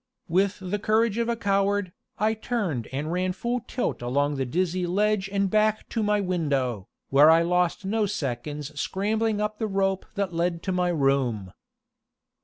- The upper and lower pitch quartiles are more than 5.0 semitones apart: Yes, wide, 5.5 semitones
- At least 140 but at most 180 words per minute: Yes, average, 170 wpm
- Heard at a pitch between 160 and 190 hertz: Yes, medium, 185 Hz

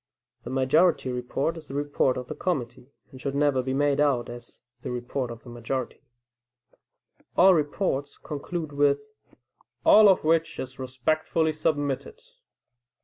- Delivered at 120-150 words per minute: Yes, average, 145 wpm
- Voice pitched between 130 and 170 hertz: Yes, medium, 140 Hz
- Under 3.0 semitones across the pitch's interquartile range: No, average, 3.4 semitones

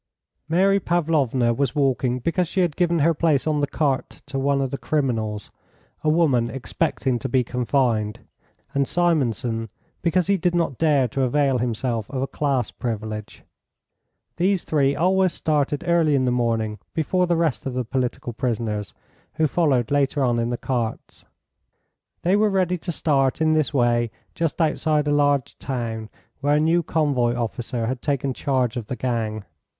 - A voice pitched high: No, low, 135 Hz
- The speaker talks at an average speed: Yes, average, 170 wpm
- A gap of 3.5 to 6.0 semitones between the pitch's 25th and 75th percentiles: Yes, average, 4.7 semitones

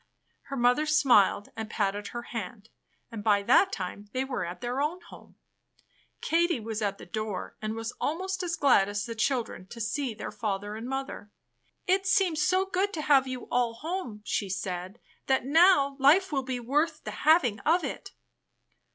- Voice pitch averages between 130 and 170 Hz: No, very high, 250 Hz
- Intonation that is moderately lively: No, wide, 6.4 semitones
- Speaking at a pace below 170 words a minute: No, average, 180 wpm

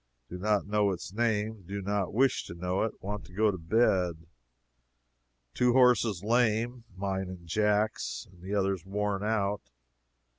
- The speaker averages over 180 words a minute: No, average, 155 wpm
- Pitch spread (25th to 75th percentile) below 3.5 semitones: Yes, narrow, 2.6 semitones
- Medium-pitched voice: No, low, 105 Hz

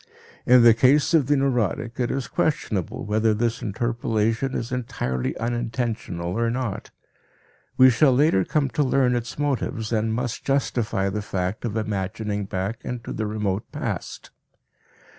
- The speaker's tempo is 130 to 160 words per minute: Yes, average, 145 wpm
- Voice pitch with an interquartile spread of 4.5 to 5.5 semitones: No, average, 3.1 semitones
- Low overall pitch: Yes, low, 115 Hz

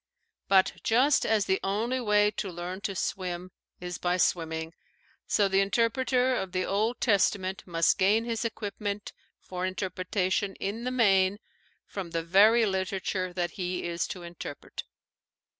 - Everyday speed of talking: Yes, average, 145 wpm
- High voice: Yes, high, 195 Hz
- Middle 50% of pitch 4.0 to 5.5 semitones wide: No, average, 2.8 semitones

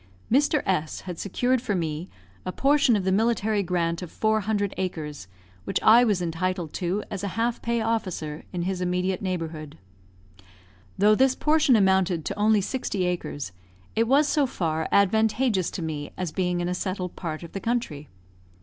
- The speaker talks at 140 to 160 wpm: No, average, 175 wpm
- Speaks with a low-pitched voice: No, high, 190 Hz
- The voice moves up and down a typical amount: Yes, average, 4.2 semitones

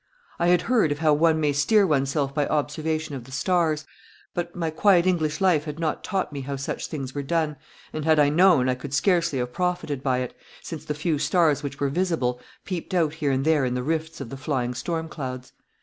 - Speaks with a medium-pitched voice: Yes, medium, 150 Hz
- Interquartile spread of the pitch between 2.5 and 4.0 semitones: Yes, average, 3.3 semitones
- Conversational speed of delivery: No, fast, 225 wpm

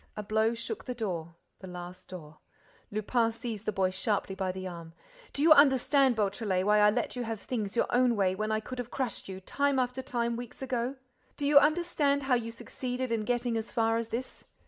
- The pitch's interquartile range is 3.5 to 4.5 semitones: Yes, average, 4.0 semitones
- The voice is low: No, high, 230 Hz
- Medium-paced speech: No, fast, 215 wpm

